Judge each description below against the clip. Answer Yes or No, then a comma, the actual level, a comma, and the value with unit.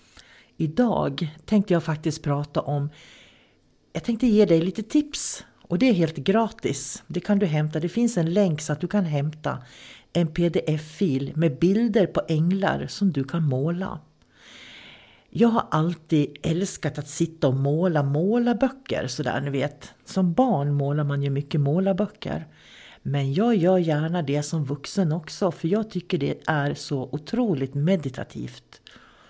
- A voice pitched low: No, medium, 165 Hz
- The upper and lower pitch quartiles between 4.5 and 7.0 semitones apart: Yes, average, 5.0 semitones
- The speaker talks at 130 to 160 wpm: Yes, average, 155 wpm